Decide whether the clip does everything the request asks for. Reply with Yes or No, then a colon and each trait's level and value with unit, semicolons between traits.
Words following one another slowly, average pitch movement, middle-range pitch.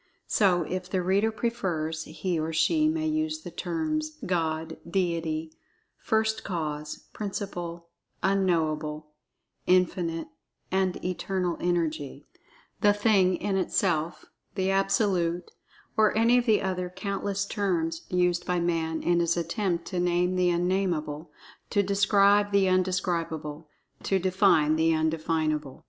Yes: slow, 130 wpm; average, 3.3 semitones; medium, 180 Hz